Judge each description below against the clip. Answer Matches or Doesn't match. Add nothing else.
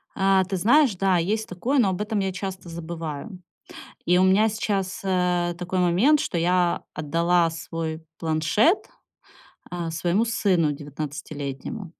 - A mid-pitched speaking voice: Matches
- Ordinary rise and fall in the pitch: Matches